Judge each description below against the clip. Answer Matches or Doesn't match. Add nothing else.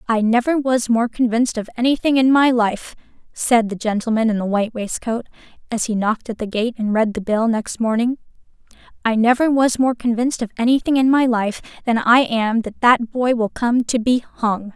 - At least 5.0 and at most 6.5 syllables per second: Matches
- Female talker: Matches